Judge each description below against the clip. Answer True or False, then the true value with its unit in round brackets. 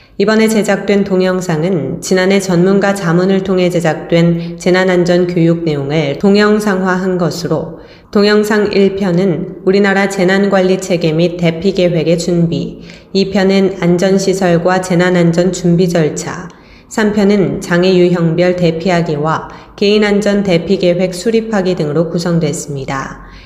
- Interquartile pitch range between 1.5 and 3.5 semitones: True (2.4 semitones)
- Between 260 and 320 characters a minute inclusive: True (285 characters per minute)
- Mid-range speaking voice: True (180 Hz)